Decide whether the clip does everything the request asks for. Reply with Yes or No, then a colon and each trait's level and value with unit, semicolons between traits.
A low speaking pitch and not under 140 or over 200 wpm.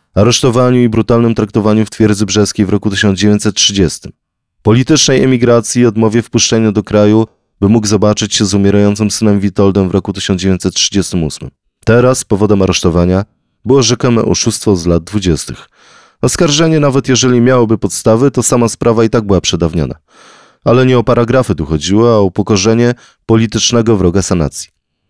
Yes: low, 110 Hz; average, 145 wpm